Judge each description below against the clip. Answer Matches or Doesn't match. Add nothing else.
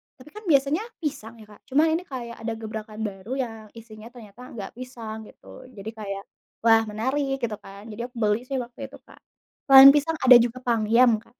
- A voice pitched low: Doesn't match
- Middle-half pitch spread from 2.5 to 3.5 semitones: Matches